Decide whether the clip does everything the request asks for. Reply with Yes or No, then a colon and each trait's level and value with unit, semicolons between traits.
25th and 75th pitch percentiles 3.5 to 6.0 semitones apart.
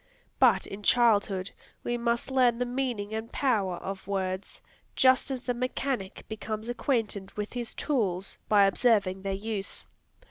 Yes: average, 3.8 semitones